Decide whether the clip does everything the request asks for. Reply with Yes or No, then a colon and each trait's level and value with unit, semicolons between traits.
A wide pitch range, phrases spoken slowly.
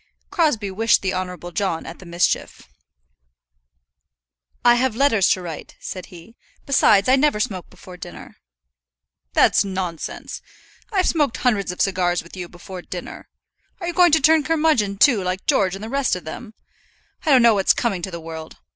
No: wide, 6.1 semitones; average, 175 wpm